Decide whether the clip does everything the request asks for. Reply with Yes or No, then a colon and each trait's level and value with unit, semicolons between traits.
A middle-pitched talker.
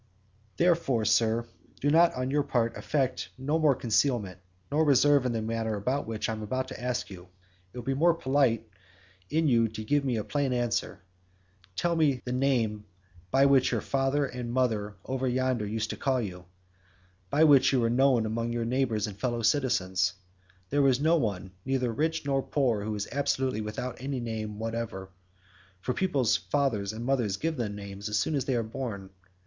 No: low, 125 Hz